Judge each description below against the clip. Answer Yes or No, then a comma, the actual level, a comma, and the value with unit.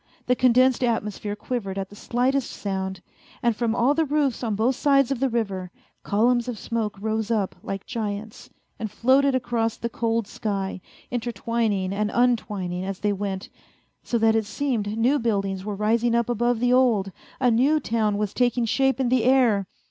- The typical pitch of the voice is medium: No, high, 230 Hz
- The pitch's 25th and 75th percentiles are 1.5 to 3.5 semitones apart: Yes, average, 3.2 semitones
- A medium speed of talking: Yes, average, 180 wpm